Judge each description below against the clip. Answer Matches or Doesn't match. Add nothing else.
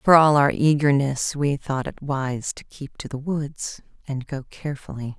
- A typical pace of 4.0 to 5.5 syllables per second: Matches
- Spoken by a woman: Matches